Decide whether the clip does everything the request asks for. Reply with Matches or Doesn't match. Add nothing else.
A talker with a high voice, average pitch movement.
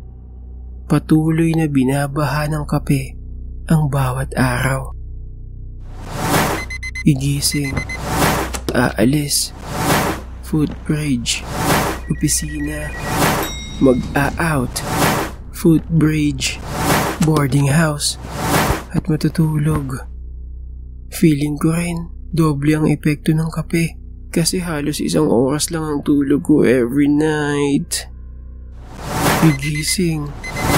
Doesn't match